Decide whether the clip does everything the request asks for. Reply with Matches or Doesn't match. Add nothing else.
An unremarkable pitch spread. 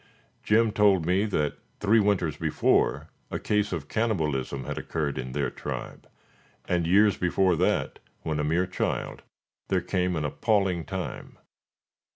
Matches